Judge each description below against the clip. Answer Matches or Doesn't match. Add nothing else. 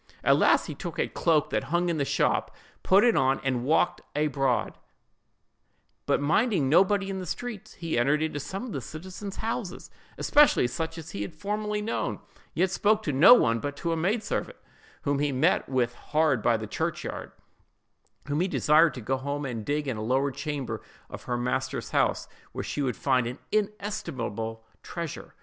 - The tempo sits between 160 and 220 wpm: Matches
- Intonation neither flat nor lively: Doesn't match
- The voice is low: Doesn't match